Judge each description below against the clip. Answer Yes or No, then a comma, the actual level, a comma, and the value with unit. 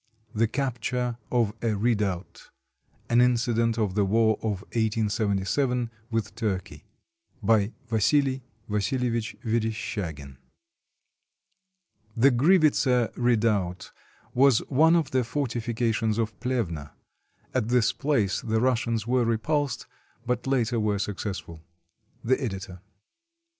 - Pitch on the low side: Yes, low, 115 Hz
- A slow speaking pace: Yes, slow, 105 wpm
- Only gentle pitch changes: No, average, 3.0 semitones